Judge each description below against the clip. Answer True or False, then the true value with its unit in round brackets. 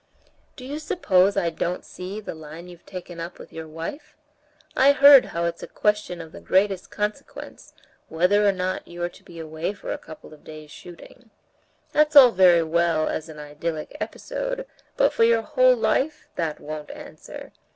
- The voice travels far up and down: True (5.8 semitones)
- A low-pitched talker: False (180 Hz)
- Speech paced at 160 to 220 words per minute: True (180 wpm)